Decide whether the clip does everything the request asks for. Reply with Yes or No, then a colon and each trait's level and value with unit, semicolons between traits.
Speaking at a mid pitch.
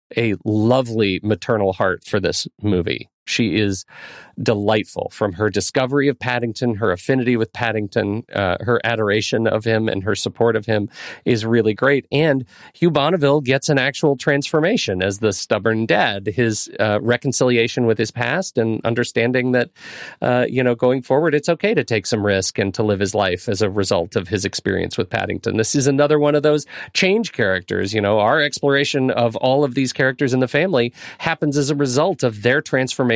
No: low, 120 Hz